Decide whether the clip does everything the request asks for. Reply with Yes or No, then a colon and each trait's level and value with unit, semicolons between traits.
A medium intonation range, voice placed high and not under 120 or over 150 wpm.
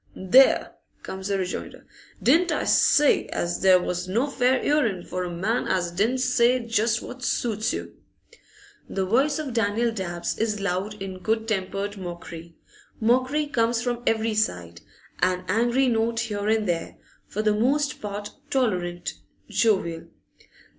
Yes: average, 4.5 semitones; high, 215 Hz; average, 145 wpm